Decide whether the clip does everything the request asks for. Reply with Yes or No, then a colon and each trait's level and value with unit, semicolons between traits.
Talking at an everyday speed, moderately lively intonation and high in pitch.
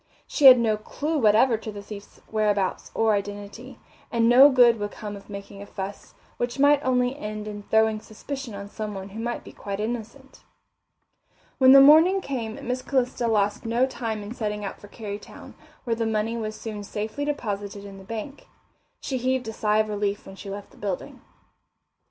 Yes: average, 185 wpm; average, 3.4 semitones; high, 220 Hz